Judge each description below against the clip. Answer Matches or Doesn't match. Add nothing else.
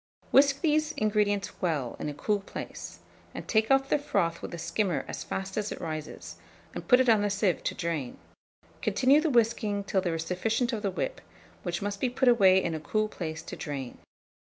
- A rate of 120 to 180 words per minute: Doesn't match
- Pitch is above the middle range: Matches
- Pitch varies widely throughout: Matches